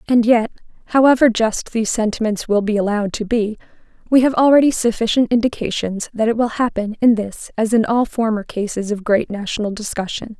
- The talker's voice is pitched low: No, high, 225 Hz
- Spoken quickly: No, average, 180 wpm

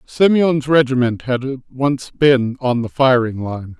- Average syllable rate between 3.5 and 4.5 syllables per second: Yes, 3.6 syllables/s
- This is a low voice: Yes, low, 130 Hz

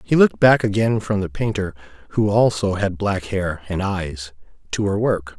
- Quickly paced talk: No, average, 190 wpm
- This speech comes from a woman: No, male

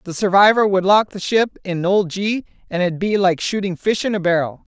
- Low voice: No, high, 190 Hz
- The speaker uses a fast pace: Yes, fast, 225 wpm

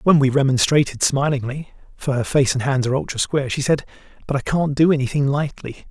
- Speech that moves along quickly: No, average, 185 wpm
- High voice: No, medium, 140 Hz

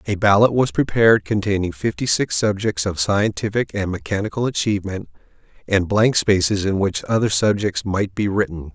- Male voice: Yes, male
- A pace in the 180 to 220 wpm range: No, average, 160 wpm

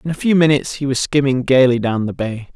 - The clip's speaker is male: Yes, male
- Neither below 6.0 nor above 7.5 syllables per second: Yes, 6.2 syllables/s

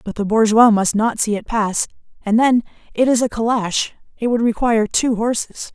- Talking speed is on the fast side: No, average, 190 wpm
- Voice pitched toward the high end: Yes, high, 225 Hz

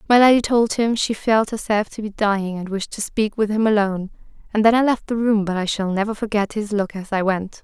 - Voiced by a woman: Yes, female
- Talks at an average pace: No, fast, 260 wpm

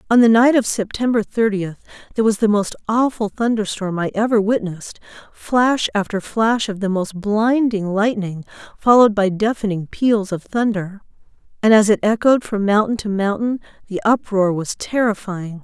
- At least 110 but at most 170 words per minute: Yes, average, 155 wpm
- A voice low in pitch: No, high, 210 Hz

